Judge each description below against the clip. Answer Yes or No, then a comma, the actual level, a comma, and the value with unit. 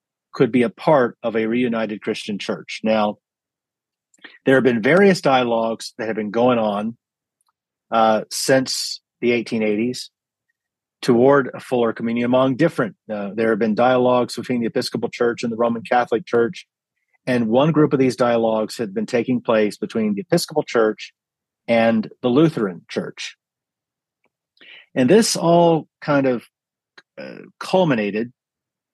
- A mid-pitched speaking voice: No, low, 120 Hz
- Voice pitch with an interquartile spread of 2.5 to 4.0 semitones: Yes, average, 3.0 semitones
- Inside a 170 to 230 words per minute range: No, average, 145 wpm